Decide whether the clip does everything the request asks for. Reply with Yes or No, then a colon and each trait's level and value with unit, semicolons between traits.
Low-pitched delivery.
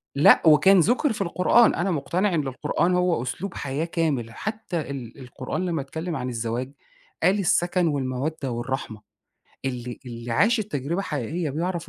No: medium, 155 Hz